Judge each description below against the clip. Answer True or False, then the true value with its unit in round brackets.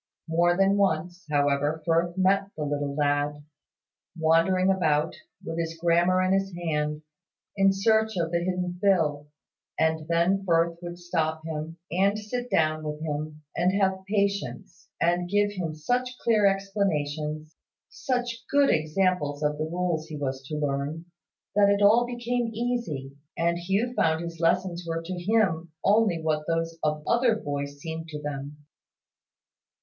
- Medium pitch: True (170 Hz)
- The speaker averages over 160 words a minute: False (150 wpm)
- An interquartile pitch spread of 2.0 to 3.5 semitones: False (4.1 semitones)